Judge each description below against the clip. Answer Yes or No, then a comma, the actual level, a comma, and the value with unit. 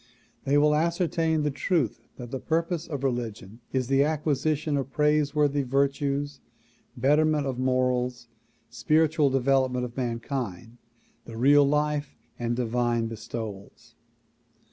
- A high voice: No, low, 135 Hz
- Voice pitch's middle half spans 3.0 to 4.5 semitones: Yes, average, 3.4 semitones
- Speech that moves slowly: Yes, slow, 120 wpm